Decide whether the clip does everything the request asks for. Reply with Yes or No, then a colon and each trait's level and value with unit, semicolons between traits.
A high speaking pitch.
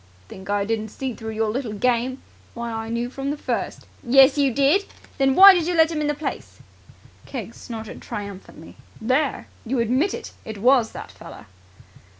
Yes: high, 245 Hz